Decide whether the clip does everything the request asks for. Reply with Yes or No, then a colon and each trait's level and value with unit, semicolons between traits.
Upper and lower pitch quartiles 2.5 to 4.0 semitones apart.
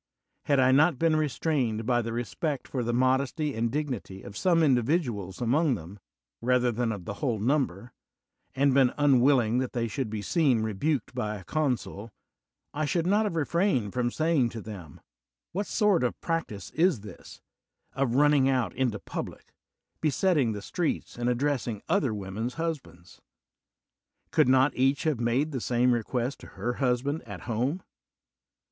No: average, 4.5 semitones